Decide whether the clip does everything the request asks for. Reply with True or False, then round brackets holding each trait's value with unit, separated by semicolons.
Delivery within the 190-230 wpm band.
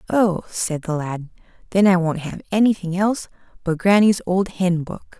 False (175 wpm)